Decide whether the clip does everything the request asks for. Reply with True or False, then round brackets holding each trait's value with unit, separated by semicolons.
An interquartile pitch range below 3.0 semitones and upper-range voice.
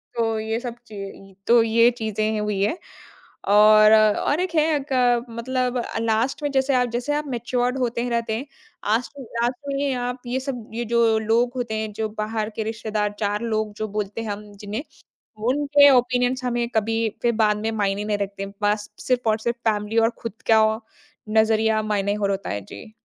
True (2.6 semitones; 225 Hz)